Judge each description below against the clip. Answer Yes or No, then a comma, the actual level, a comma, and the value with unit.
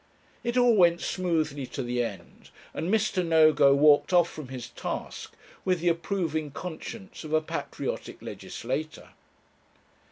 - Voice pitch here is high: No, medium, 160 Hz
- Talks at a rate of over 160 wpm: No, slow, 135 wpm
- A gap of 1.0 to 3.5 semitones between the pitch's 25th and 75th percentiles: No, average, 3.9 semitones